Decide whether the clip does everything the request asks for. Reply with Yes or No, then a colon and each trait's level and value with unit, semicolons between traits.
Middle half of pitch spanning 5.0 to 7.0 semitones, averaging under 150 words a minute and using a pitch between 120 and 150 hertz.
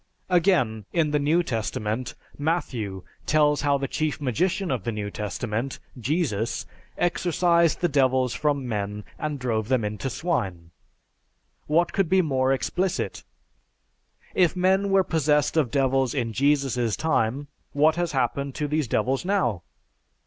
Yes: wide, 5.5 semitones; average, 140 wpm; medium, 140 Hz